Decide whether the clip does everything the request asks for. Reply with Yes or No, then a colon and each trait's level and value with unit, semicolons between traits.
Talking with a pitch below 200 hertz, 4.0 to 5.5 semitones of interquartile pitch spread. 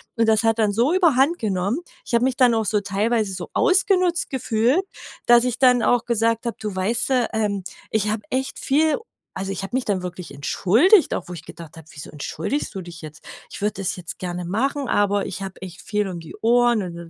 No: high, 220 Hz; average, 4.9 semitones